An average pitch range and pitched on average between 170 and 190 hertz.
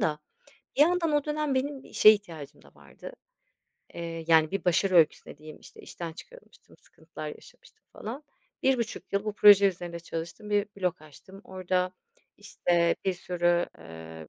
Yes: average, 4.3 semitones; medium, 185 Hz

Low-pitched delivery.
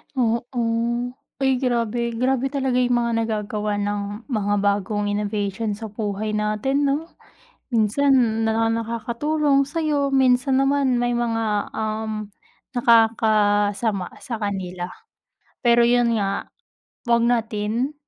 No: high, 230 Hz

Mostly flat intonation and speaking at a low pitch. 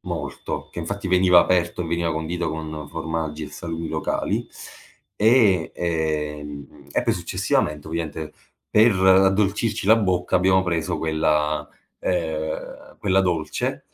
No: average, 3.1 semitones; very low, 85 Hz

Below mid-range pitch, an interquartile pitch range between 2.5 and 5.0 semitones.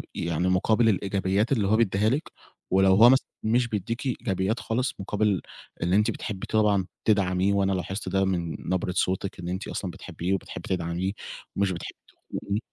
Yes: very low, 95 Hz; average, 2.8 semitones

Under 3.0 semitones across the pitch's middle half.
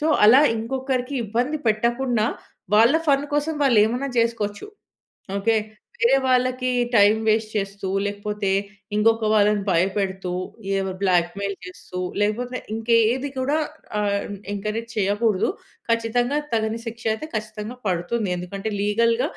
No: average, 3.3 semitones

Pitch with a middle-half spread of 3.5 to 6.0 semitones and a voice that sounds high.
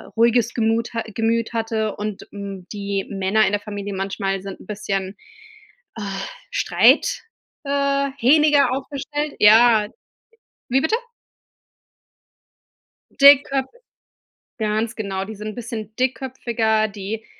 Yes: average, 3.8 semitones; high, 220 Hz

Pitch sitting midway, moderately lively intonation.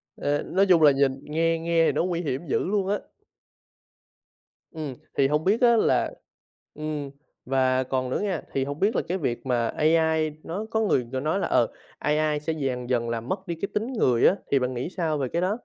Yes: medium, 155 Hz; average, 5.0 semitones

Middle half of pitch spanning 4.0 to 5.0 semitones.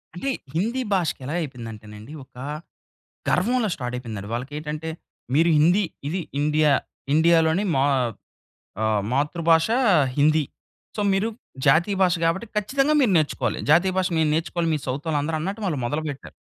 Yes: average, 4.6 semitones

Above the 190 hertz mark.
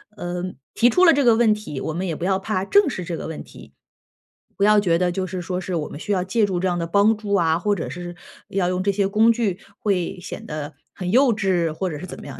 No: medium, 185 Hz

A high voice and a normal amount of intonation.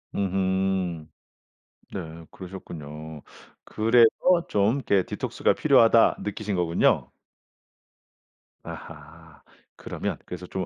No: very low, 95 Hz; average, 3.5 semitones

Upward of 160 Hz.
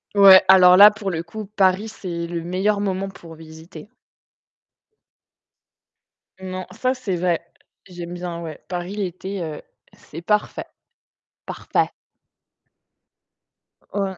Yes: medium, 185 Hz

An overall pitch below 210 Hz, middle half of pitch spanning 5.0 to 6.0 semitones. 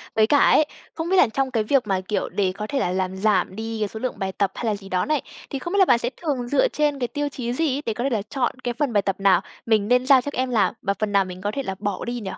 No: high, 230 Hz; average, 5.3 semitones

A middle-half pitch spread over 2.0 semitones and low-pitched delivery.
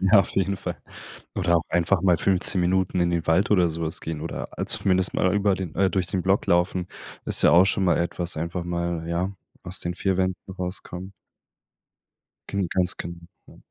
No: narrow, 1.6 semitones; very low, 90 Hz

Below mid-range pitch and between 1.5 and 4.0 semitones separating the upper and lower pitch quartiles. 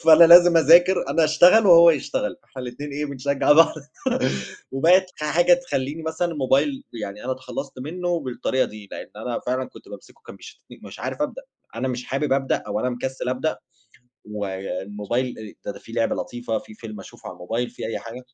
No: low, 130 Hz; average, 5.3 semitones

